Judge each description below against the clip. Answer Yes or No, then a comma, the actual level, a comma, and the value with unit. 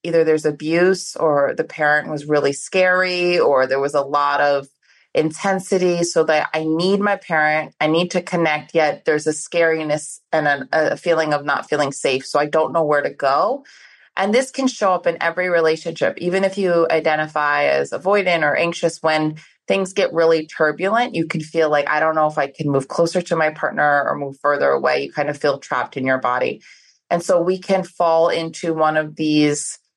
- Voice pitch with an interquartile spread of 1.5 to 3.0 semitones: Yes, narrow, 2.6 semitones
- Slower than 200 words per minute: No, fast, 205 wpm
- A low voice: No, medium, 160 Hz